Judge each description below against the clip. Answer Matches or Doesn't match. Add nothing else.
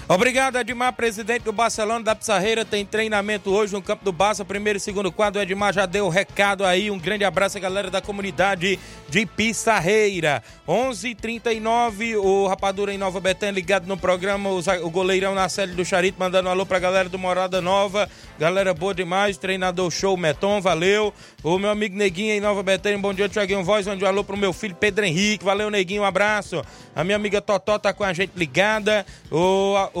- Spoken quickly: Matches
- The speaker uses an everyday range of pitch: Doesn't match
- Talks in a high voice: Matches